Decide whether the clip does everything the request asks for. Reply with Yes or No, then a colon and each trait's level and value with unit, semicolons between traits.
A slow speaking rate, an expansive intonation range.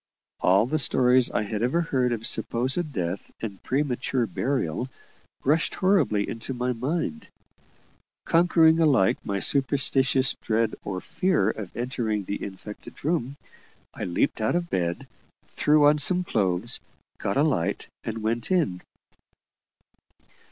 Yes: slow, 130 wpm; wide, 5.7 semitones